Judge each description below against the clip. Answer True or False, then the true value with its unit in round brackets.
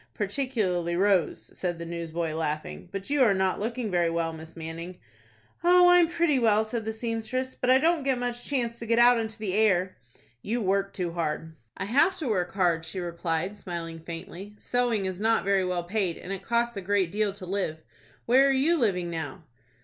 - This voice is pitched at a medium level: False (200 Hz)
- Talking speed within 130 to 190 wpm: False (200 wpm)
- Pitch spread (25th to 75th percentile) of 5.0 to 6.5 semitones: True (5.5 semitones)